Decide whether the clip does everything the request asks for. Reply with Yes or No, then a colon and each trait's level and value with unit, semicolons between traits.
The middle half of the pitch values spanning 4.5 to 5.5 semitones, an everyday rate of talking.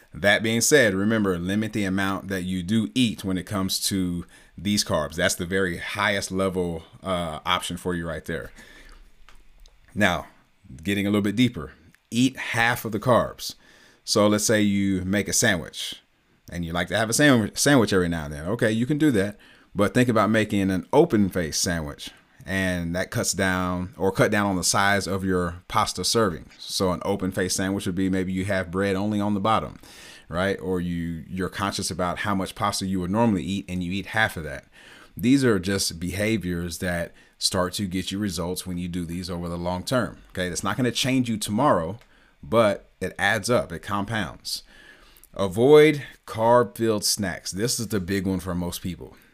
No: average, 2.8 semitones; average, 195 wpm